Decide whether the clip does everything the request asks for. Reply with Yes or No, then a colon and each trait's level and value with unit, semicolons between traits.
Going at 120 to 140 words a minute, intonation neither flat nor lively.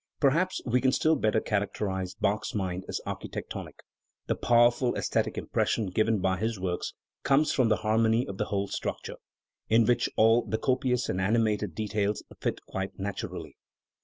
No: average, 160 wpm; average, 3.4 semitones